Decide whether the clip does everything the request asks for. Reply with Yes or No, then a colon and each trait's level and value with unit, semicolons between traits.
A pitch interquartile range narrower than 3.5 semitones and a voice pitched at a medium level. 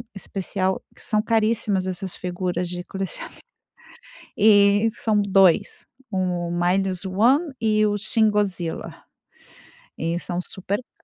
No: average, 2.8 semitones; high, 195 Hz